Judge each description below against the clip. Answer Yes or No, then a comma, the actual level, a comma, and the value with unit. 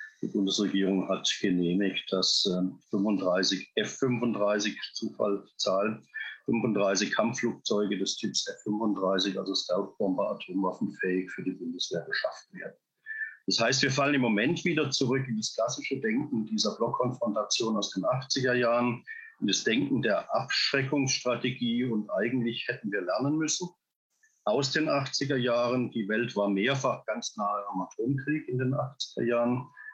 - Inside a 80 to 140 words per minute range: Yes, average, 135 wpm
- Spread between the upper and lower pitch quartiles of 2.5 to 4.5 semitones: No, average, 5.3 semitones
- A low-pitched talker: Yes, low, 120 Hz